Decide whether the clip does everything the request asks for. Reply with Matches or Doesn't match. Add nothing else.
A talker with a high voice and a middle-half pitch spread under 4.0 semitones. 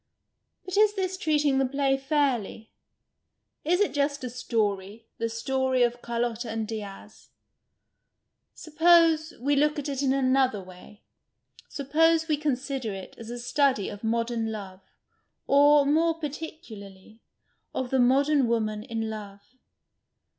Doesn't match